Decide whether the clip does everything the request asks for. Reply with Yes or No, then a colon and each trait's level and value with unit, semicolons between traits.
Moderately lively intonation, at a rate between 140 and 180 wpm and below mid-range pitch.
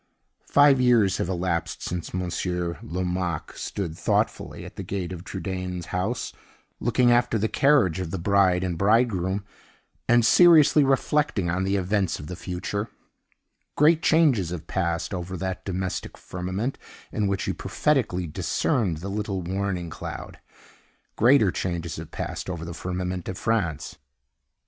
Yes: average, 3.9 semitones; average, 145 wpm; very low, 95 Hz